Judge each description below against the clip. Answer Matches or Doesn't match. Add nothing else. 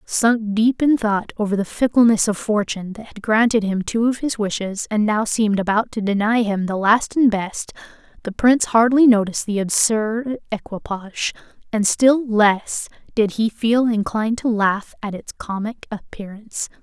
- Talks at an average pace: Matches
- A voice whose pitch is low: Doesn't match